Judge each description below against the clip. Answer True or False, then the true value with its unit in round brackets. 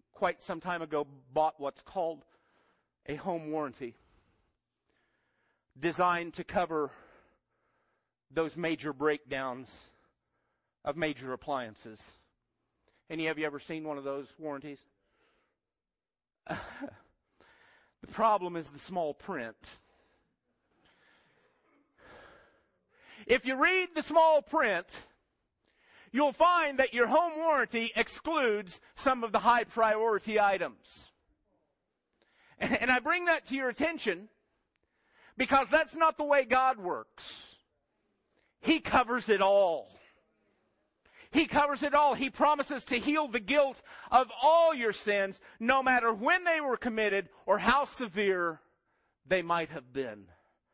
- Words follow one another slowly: True (115 wpm)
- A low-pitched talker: False (210 Hz)